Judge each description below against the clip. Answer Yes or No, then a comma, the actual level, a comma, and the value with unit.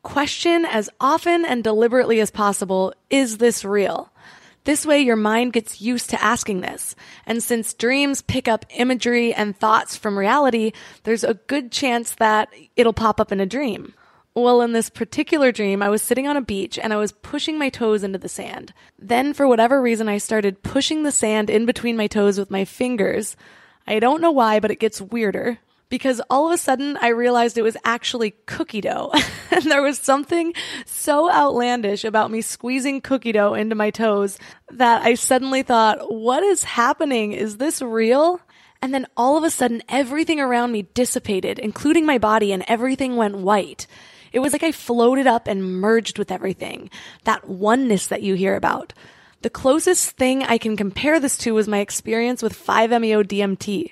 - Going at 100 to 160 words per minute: No, average, 185 wpm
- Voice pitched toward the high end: Yes, high, 235 Hz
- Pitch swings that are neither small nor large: Yes, average, 3.8 semitones